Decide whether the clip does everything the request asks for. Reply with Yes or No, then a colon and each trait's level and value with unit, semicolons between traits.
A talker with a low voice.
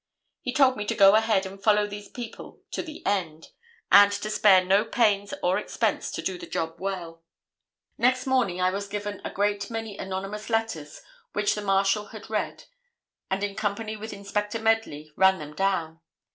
No: high, 205 Hz